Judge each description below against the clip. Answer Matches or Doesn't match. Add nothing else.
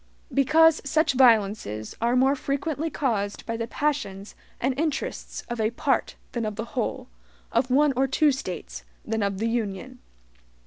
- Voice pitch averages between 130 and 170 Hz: Doesn't match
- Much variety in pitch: Doesn't match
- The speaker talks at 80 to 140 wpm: Doesn't match